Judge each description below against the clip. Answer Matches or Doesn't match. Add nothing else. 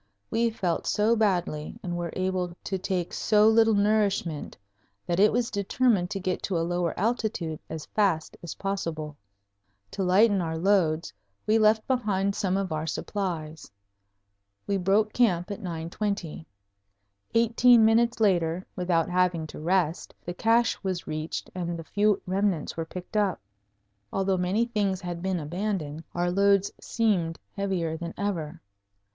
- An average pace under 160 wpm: Matches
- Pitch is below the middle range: Doesn't match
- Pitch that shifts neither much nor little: Matches